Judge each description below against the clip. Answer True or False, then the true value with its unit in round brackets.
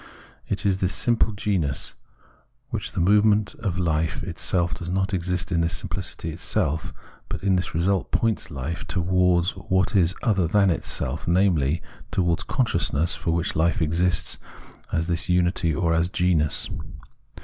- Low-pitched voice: True (90 Hz)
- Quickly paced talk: False (155 wpm)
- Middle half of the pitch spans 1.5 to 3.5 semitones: True (2.4 semitones)